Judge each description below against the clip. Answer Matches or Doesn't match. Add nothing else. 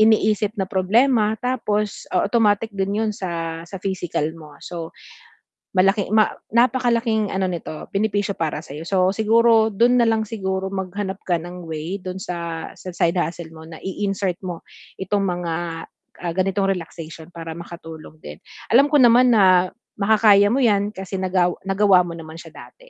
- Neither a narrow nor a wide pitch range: Matches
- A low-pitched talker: Doesn't match